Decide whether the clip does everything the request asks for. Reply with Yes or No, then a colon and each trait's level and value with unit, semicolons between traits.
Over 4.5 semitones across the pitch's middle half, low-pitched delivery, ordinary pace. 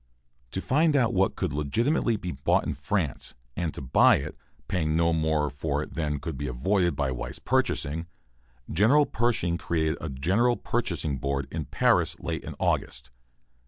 Yes: average, 5.3 semitones; very low, 80 Hz; average, 165 wpm